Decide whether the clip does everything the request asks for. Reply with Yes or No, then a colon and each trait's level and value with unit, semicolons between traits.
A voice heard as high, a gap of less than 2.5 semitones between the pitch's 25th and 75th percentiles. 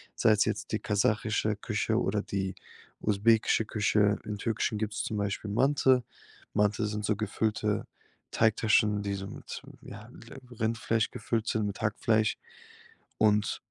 No: low, 105 Hz; narrow, 1.3 semitones